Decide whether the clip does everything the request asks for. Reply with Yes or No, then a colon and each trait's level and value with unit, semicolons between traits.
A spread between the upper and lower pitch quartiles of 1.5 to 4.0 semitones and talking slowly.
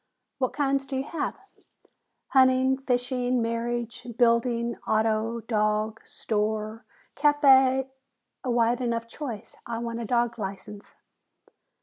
Yes: narrow, 2.5 semitones; slow, 115 wpm